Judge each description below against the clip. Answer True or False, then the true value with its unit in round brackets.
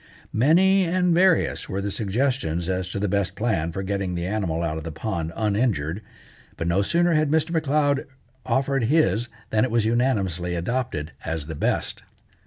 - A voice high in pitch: False (105 Hz)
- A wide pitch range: True (7.8 semitones)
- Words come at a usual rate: True (175 wpm)